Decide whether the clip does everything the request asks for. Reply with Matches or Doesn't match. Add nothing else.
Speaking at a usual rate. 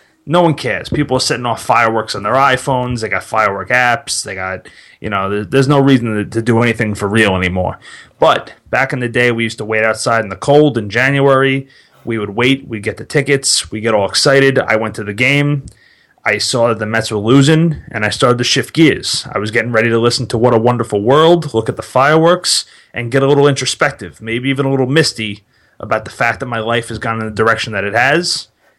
Doesn't match